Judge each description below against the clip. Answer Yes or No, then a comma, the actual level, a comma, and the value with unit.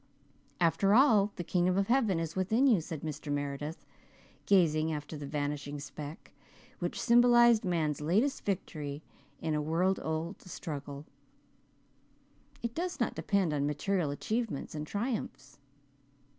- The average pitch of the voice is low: No, medium, 165 Hz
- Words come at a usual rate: No, slow, 130 wpm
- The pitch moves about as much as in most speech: No, wide, 5.7 semitones